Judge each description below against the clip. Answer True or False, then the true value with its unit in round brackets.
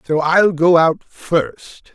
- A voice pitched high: False (165 Hz)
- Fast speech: False (155 wpm)